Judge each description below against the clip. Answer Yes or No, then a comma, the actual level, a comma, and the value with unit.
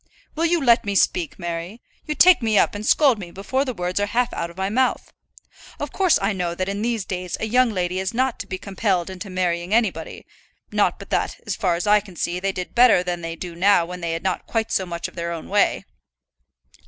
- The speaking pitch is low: No, high, 190 Hz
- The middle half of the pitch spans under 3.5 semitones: No, average, 4.2 semitones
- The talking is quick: Yes, fast, 240 wpm